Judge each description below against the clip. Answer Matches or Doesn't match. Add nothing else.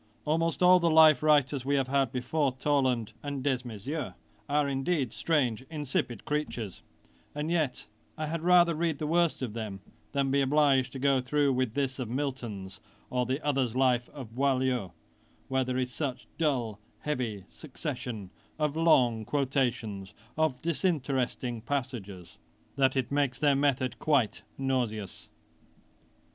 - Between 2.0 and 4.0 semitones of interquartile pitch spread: Matches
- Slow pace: Doesn't match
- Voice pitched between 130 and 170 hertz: Matches